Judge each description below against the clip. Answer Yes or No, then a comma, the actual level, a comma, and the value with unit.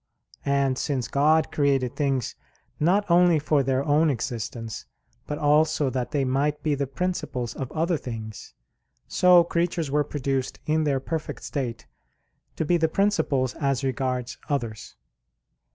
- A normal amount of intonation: Yes, average, 3.3 semitones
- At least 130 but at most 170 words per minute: Yes, average, 140 wpm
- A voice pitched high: No, medium, 140 Hz